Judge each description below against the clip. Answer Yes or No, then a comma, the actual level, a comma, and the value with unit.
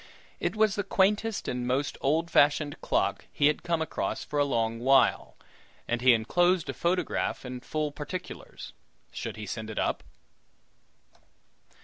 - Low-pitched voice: No, medium, 145 Hz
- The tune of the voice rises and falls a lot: Yes, wide, 5.9 semitones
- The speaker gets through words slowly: No, average, 145 wpm